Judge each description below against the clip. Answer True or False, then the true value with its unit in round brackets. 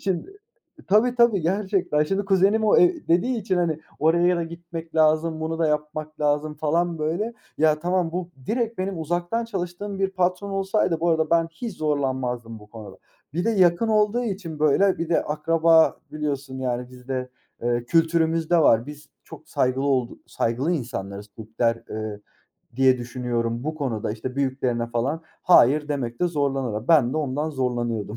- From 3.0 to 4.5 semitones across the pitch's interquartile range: False (5.5 semitones)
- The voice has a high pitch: False (155 Hz)